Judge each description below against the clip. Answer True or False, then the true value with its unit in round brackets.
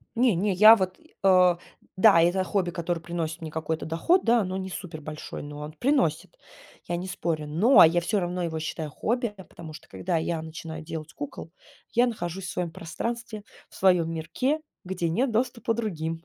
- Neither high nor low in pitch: True (175 Hz)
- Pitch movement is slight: False (4.3 semitones)